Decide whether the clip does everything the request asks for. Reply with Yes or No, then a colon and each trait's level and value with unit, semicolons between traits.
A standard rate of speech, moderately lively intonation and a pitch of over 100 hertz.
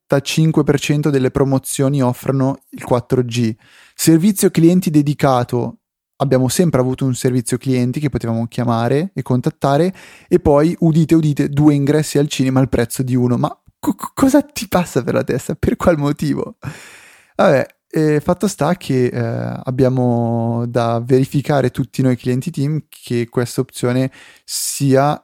Yes: average, 145 wpm; average, 3.3 semitones; low, 135 Hz